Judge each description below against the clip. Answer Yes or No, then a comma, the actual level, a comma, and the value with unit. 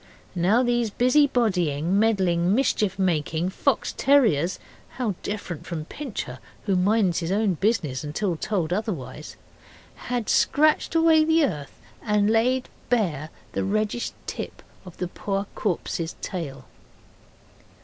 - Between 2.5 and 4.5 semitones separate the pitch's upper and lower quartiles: No, wide, 5.6 semitones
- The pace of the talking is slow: Yes, slow, 125 wpm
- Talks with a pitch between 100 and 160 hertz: No, high, 200 Hz